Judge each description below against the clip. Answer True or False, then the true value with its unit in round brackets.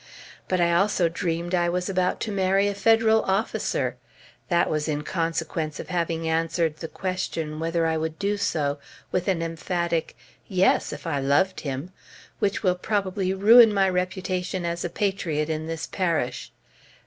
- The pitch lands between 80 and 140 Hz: False (175 Hz)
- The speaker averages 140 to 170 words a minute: True (160 wpm)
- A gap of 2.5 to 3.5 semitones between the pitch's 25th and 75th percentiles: True (2.8 semitones)